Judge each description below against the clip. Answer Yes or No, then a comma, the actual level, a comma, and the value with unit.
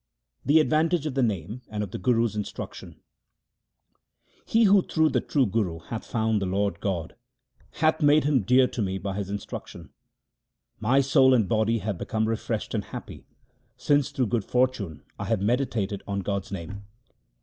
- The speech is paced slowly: No, average, 175 wpm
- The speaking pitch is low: Yes, low, 110 Hz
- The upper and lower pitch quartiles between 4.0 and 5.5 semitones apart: Yes, average, 5.1 semitones